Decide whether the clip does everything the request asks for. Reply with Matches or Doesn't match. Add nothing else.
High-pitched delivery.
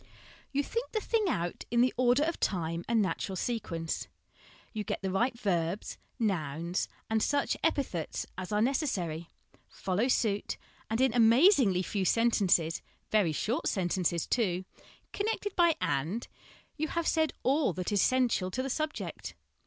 Matches